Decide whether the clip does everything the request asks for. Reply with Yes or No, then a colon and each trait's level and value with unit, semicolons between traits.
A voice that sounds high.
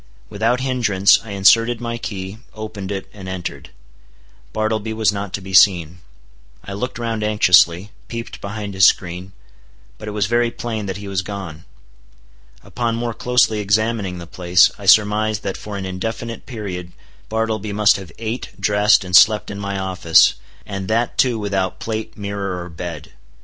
No: low, 105 Hz